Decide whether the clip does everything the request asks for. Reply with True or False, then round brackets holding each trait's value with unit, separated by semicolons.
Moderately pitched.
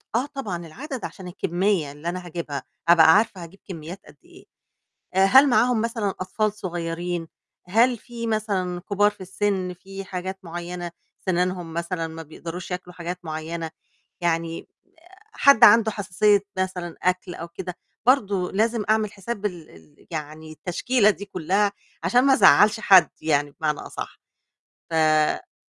True (180 Hz)